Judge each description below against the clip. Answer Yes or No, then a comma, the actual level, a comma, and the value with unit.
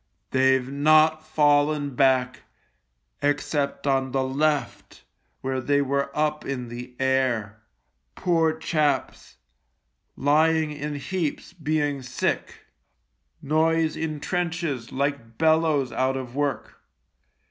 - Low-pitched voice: No, medium, 145 Hz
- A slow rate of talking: Yes, slow, 105 wpm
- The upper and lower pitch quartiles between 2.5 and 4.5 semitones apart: Yes, average, 2.8 semitones